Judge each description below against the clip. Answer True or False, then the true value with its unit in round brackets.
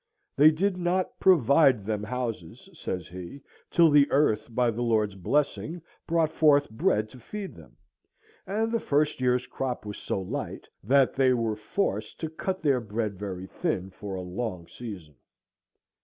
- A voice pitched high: False (125 Hz)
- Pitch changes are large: True (6.5 semitones)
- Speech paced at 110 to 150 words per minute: False (160 wpm)